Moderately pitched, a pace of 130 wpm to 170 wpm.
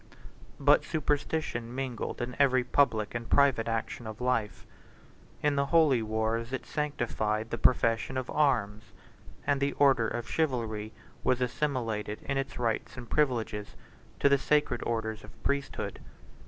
No: low, 120 Hz; average, 140 wpm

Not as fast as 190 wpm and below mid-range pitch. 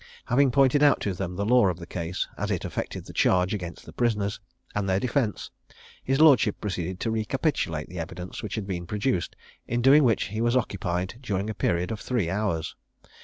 No: average, 200 wpm; low, 105 Hz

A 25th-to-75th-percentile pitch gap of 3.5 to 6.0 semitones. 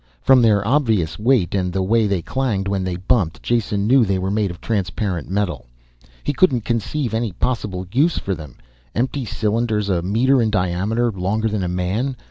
Yes: average, 4.1 semitones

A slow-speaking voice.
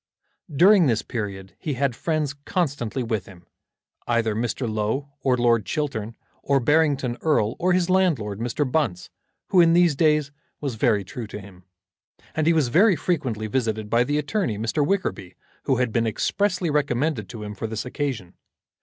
No: average, 170 wpm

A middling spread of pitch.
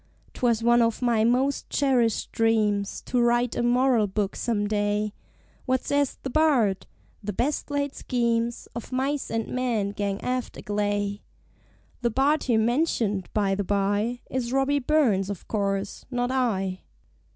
Yes: average, 3.8 semitones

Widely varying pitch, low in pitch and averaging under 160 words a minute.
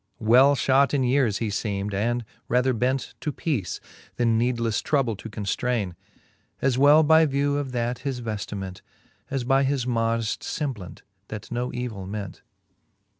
No: average, 3.8 semitones; low, 120 Hz; average, 150 wpm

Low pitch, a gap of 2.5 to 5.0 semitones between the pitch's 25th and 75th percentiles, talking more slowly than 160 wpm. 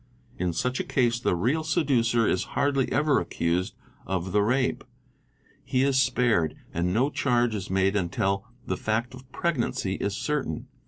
No: low, 120 Hz; wide, 5.6 semitones; average, 150 wpm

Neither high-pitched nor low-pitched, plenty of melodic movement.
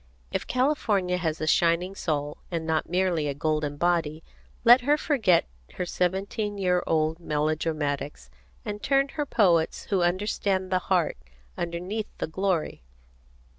No: medium, 175 Hz; average, 4.0 semitones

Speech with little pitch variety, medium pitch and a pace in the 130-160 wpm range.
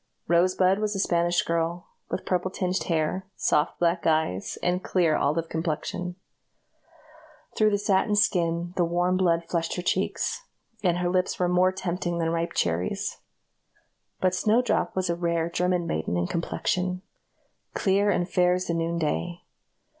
Yes: narrow, 1.6 semitones; medium, 175 Hz; average, 150 wpm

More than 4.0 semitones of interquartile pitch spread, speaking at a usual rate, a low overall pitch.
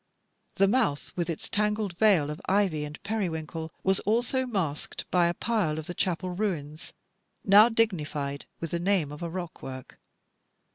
No: average, 5.0 semitones; average, 155 wpm; medium, 180 Hz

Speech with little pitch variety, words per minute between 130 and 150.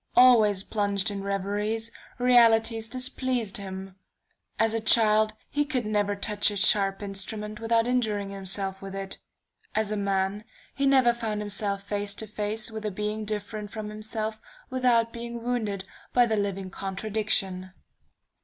Yes: narrow, 2.2 semitones; average, 145 wpm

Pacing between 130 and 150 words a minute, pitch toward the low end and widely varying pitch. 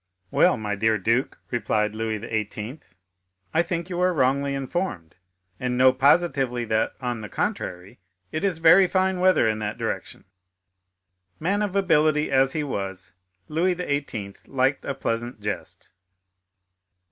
Yes: average, 140 wpm; low, 130 Hz; wide, 7.3 semitones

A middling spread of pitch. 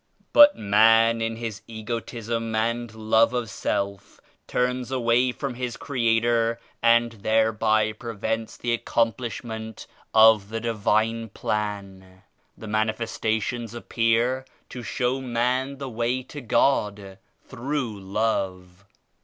No: narrow, 1.6 semitones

